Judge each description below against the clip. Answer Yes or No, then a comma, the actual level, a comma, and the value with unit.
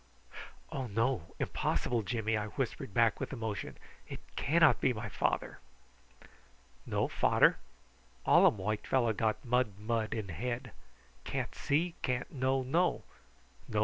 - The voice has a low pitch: Yes, low, 115 Hz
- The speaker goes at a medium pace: No, slow, 130 wpm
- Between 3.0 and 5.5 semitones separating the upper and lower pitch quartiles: Yes, average, 3.5 semitones